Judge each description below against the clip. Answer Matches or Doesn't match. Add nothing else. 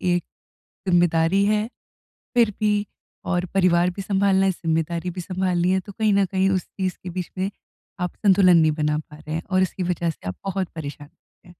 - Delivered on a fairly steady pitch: Matches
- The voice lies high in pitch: Doesn't match